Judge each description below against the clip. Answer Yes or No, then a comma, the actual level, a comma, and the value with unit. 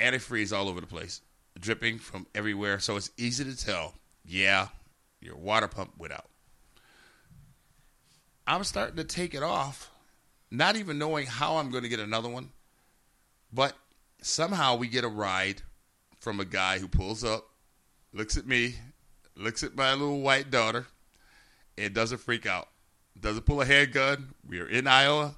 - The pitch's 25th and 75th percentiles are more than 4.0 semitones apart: Yes, wide, 5.5 semitones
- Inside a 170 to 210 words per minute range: No, average, 160 wpm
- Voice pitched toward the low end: Yes, low, 115 Hz